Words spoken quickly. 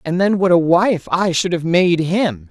Yes: fast, 240 wpm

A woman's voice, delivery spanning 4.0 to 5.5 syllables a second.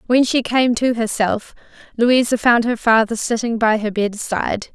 Yes: female; 4.6 syllables/s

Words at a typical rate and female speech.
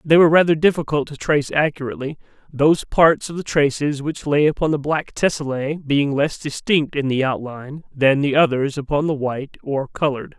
No: average, 185 wpm; male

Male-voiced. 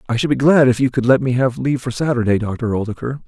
Yes: male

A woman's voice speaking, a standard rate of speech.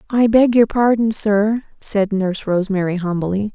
Yes: female; average, 150 wpm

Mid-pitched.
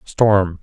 No: low, 100 Hz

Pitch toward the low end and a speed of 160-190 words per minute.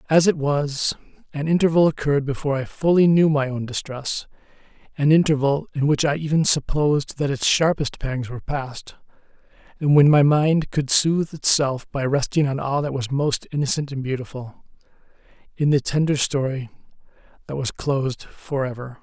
No: medium, 145 Hz; average, 165 wpm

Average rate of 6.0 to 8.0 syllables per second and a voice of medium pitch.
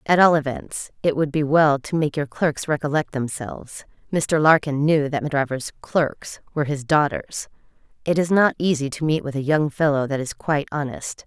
No: 4.5 syllables/s; medium, 150 Hz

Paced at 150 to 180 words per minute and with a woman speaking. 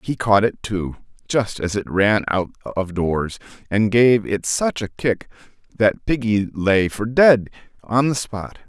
No: average, 175 wpm; male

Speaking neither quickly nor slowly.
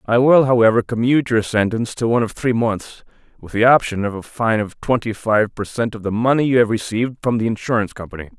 No: fast, 230 wpm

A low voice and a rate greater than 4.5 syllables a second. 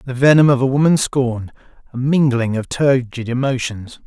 Yes: low, 130 Hz; 5.1 syllables/s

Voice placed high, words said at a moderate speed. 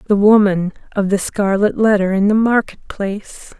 Yes: high, 200 Hz; average, 150 wpm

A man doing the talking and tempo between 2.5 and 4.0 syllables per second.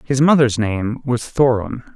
Yes: male; 3.9 syllables/s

